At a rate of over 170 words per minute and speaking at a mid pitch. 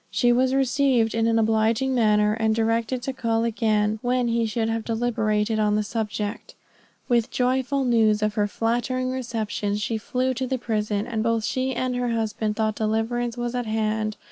No: average, 185 wpm; high, 225 Hz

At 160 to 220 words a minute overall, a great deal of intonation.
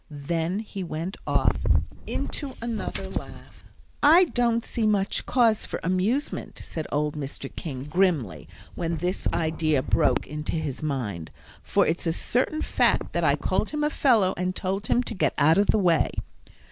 Yes: average, 165 wpm; wide, 6.0 semitones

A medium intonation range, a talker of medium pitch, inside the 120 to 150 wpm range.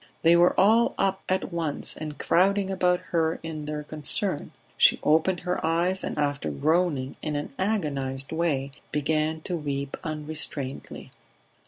Yes: average, 3.4 semitones; medium, 160 Hz; average, 145 wpm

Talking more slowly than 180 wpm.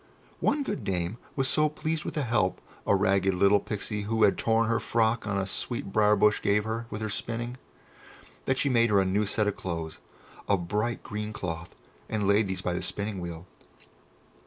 No: average, 200 wpm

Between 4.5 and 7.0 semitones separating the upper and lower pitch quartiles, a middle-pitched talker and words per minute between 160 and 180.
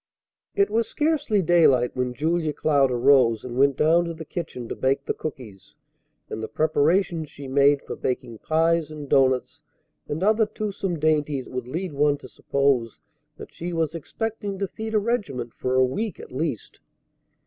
Yes: average, 5.1 semitones; medium, 150 Hz; average, 170 wpm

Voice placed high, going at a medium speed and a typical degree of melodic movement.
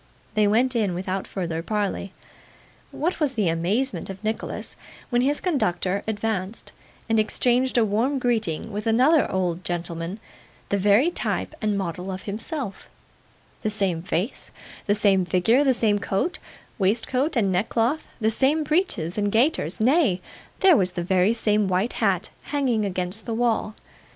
Yes: high, 215 Hz; average, 150 wpm; average, 4.6 semitones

